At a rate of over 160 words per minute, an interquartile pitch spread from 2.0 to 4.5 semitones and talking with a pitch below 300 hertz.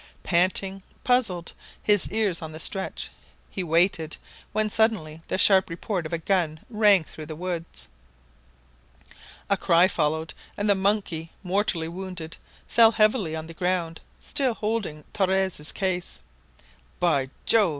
No: slow, 135 wpm; average, 3.9 semitones; medium, 185 Hz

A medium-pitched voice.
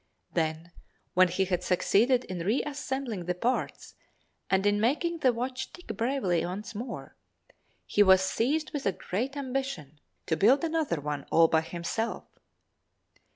No: high, 210 Hz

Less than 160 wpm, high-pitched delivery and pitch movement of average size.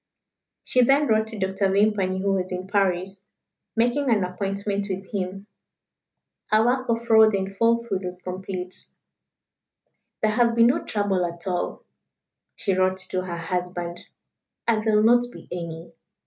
Yes: average, 150 wpm; high, 195 Hz; average, 3.2 semitones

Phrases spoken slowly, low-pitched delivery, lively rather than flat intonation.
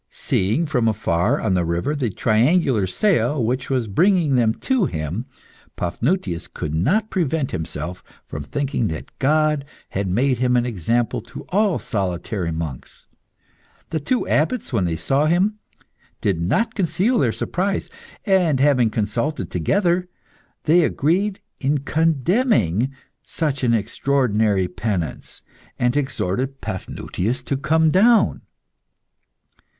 Yes: slow, 125 wpm; low, 130 Hz; wide, 8.1 semitones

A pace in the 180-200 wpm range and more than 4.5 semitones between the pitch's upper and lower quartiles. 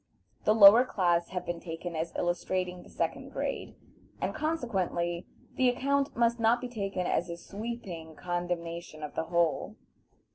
No: average, 150 wpm; average, 5.3 semitones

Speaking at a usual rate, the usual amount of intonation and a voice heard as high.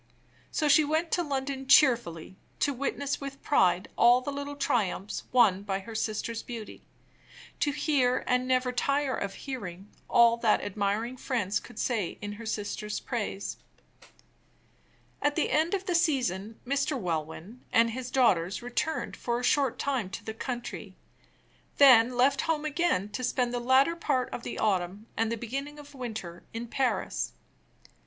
Yes: average, 160 wpm; average, 4.8 semitones; high, 245 Hz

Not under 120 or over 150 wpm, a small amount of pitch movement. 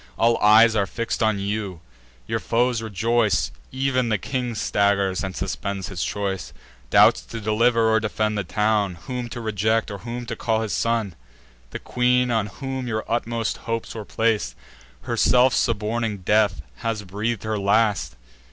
No: average, 160 wpm; narrow, 2.3 semitones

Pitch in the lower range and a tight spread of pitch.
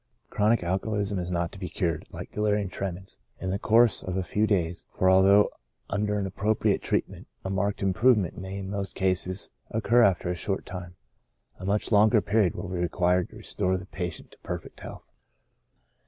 Yes: very low, 95 Hz; narrow, 2.3 semitones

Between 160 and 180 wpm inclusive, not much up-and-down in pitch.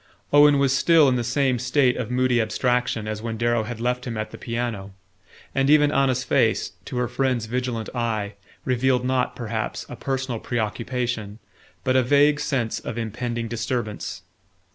Yes: average, 165 wpm; narrow, 2.2 semitones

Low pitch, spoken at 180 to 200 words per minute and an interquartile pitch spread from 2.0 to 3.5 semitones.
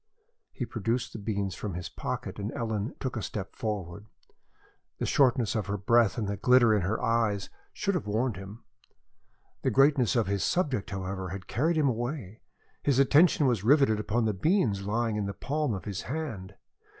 No: low, 110 Hz; average, 185 wpm; average, 4.4 semitones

